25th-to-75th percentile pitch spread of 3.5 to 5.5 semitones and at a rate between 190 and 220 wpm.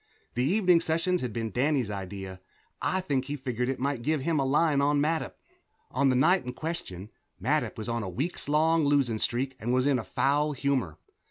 Yes: average, 4.1 semitones; average, 195 wpm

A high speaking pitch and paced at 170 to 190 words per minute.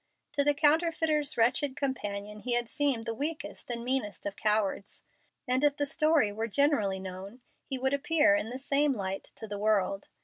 Yes: very high, 250 Hz; average, 180 wpm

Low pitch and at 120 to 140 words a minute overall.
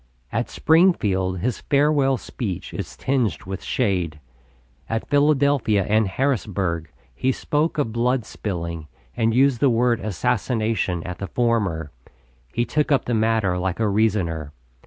Yes: low, 110 Hz; slow, 135 wpm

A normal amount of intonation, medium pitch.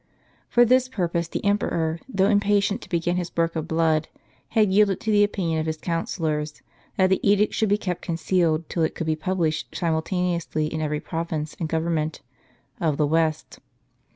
Yes: average, 3.6 semitones; medium, 170 Hz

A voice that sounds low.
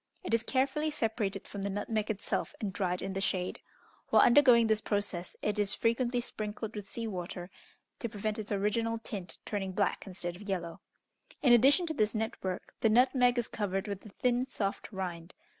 No: high, 210 Hz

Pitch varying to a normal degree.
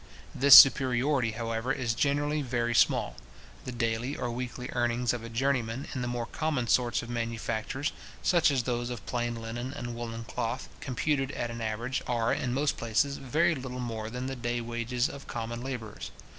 No: narrow, 2.2 semitones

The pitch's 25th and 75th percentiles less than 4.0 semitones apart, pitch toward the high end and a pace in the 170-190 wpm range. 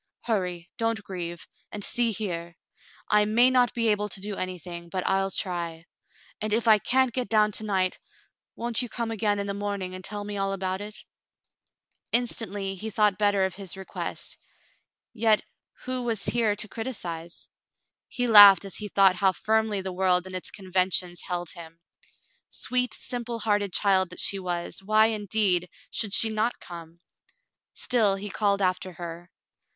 Yes: average, 3.0 semitones; high, 200 Hz; average, 175 wpm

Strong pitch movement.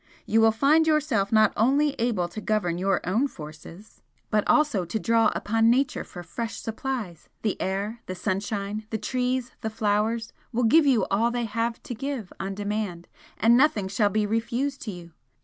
No: average, 3.4 semitones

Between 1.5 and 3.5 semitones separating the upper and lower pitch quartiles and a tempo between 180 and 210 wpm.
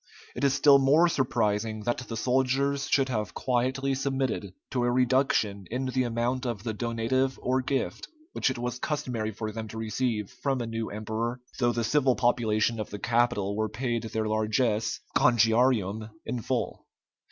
No: average, 3.1 semitones; average, 170 wpm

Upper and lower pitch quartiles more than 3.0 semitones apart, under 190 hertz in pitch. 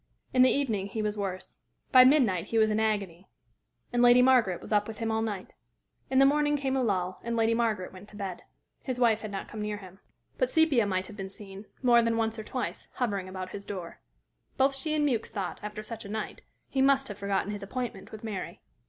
No: average, 4.0 semitones; high, 220 Hz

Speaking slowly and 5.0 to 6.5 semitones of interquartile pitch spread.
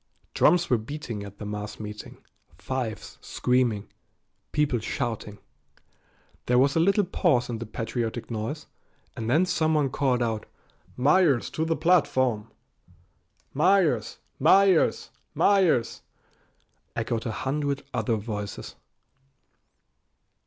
Yes: slow, 110 wpm; wide, 5.6 semitones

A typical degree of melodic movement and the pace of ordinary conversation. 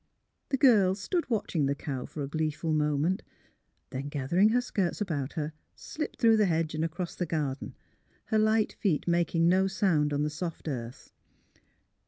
Yes: average, 4.9 semitones; average, 170 wpm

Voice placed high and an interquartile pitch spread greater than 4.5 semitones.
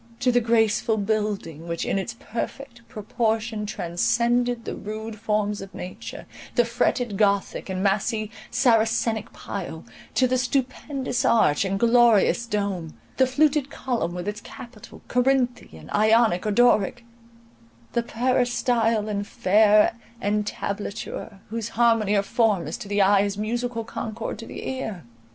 No: high, 220 Hz; average, 2.9 semitones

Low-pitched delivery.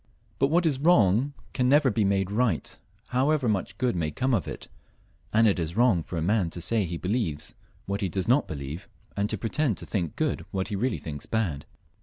Yes: low, 105 Hz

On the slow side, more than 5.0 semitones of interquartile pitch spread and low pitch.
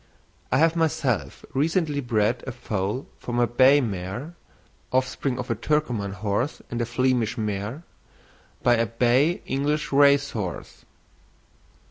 No: slow, 130 wpm; average, 4.3 semitones; low, 125 Hz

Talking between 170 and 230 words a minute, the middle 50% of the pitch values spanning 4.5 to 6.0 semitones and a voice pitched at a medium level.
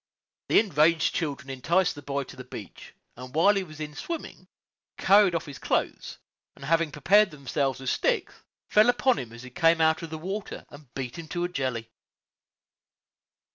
Yes: average, 180 wpm; average, 4.8 semitones; medium, 155 Hz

